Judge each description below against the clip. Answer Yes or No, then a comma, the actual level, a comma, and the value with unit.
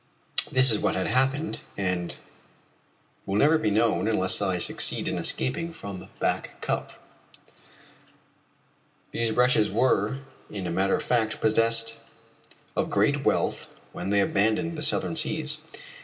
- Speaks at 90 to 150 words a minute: Yes, average, 140 wpm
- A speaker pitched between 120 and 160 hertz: No, low, 110 Hz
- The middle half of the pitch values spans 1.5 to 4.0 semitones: No, average, 4.9 semitones